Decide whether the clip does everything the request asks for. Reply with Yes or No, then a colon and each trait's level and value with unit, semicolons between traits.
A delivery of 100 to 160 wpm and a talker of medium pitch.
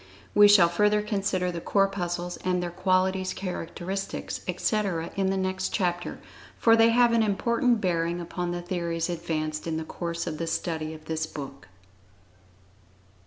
Yes: average, 155 wpm; medium, 180 Hz